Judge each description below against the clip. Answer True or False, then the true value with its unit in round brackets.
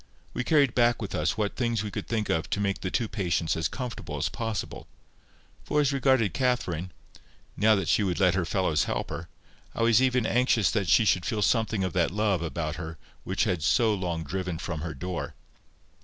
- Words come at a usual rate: False (210 wpm)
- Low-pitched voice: True (100 Hz)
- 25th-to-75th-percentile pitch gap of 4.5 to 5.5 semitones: True (4.9 semitones)